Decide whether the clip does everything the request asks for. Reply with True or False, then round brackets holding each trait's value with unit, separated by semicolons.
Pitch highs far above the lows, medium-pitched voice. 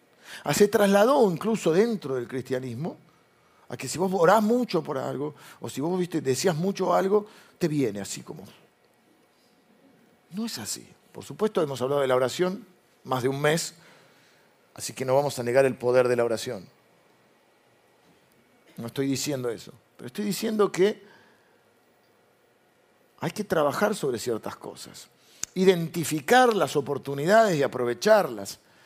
True (7.6 semitones; 165 Hz)